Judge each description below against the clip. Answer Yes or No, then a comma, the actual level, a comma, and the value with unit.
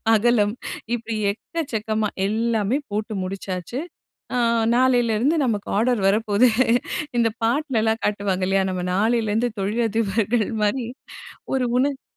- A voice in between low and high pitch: No, high, 220 Hz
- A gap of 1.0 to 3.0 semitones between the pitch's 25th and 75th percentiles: Yes, average, 2.7 semitones